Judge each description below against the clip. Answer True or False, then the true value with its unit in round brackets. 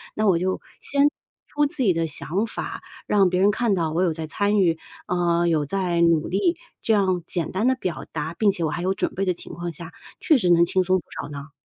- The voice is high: False (180 Hz)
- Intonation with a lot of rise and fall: False (3.3 semitones)